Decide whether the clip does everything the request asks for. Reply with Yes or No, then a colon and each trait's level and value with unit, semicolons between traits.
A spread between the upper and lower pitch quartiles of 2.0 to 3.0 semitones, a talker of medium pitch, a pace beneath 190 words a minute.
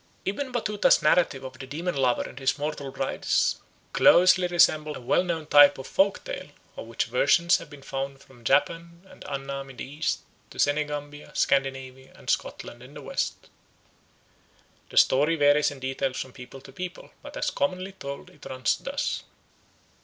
No: average, 4.2 semitones; medium, 145 Hz; average, 170 wpm